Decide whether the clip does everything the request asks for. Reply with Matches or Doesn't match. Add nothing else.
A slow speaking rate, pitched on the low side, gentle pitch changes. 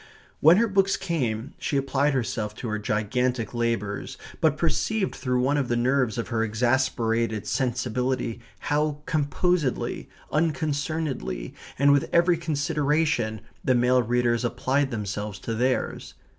Doesn't match